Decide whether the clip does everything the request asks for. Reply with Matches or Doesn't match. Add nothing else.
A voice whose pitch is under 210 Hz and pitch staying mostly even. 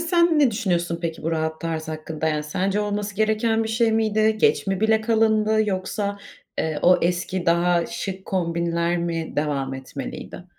Doesn't match